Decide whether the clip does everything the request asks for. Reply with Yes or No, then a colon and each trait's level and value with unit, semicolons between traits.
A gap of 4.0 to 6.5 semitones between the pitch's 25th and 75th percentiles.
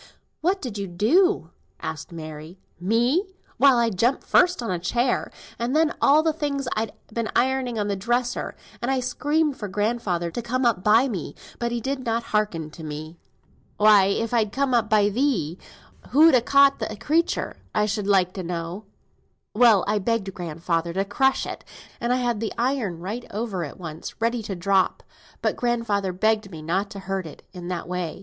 Yes: average, 5.1 semitones